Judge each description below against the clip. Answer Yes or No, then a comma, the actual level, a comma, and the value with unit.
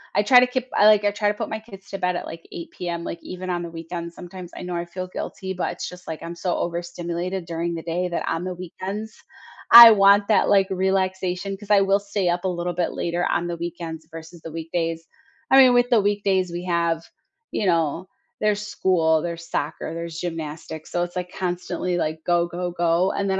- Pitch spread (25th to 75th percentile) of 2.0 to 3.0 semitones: Yes, narrow, 2.4 semitones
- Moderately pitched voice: Yes, medium, 180 Hz